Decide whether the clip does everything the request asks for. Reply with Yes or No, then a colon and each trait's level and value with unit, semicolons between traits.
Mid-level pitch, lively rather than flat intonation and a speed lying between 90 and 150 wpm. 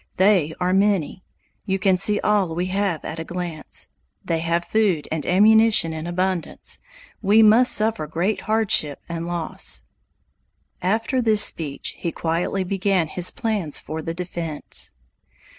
No: medium, 180 Hz; average, 4.0 semitones; average, 140 wpm